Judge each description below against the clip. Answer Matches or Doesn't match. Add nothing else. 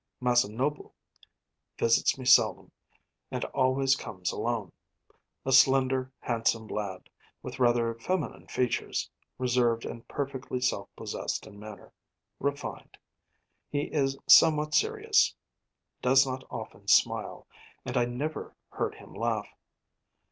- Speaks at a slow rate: Matches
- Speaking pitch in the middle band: Doesn't match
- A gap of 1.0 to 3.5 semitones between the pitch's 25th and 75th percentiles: Matches